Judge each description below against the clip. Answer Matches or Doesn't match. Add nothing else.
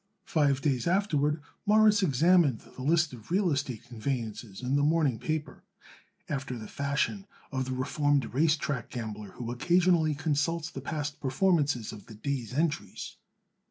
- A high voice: Doesn't match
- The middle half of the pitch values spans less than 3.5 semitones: Doesn't match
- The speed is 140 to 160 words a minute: Matches